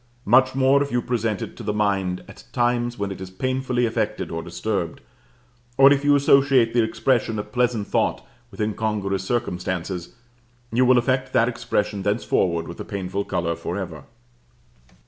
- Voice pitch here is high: No, low, 110 Hz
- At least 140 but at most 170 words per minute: Yes, average, 165 wpm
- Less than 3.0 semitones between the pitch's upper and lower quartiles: No, average, 4.3 semitones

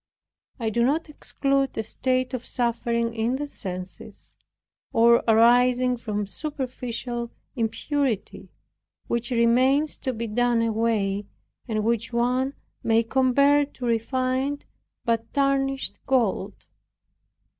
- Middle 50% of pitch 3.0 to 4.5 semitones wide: No, narrow, 2.5 semitones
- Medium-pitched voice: No, high, 240 Hz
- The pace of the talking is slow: Yes, slow, 110 wpm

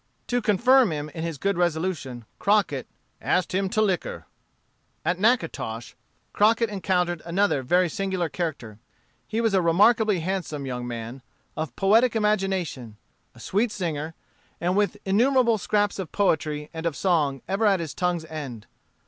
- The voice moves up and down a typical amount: Yes, average, 4.9 semitones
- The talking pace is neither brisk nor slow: Yes, average, 150 wpm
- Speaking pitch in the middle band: Yes, medium, 180 Hz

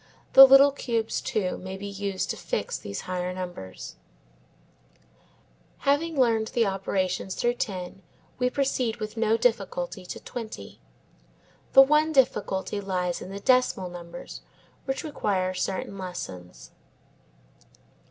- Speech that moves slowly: Yes, slow, 125 wpm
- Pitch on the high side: Yes, high, 200 Hz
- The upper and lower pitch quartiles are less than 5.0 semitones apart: No, average, 5.3 semitones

